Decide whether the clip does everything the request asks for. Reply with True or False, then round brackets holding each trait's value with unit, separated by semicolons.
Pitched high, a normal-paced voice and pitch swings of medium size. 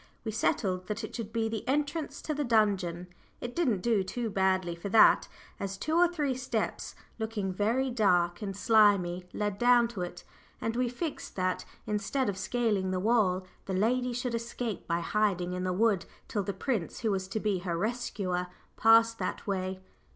True (210 Hz; 180 wpm; 4.1 semitones)